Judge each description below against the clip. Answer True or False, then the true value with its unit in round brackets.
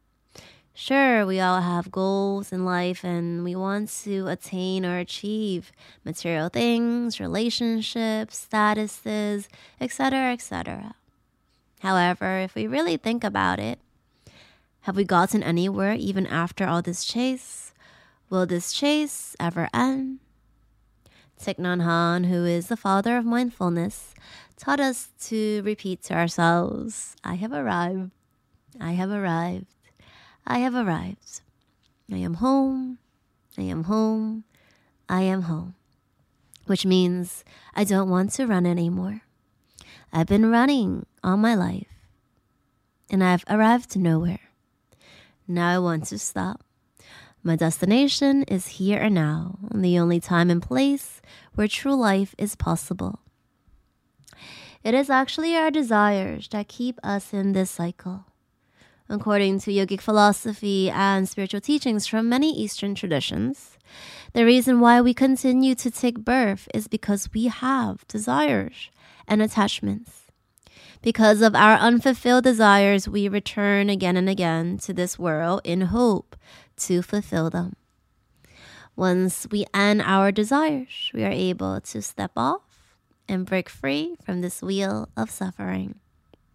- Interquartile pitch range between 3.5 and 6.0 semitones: True (4.3 semitones)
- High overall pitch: True (195 Hz)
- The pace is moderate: False (130 wpm)